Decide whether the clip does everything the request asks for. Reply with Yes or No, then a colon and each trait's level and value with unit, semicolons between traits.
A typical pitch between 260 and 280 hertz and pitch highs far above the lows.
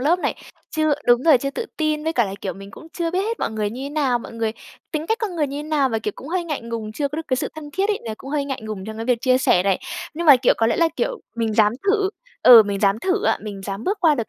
Yes: very high, 270 Hz; wide, 6.3 semitones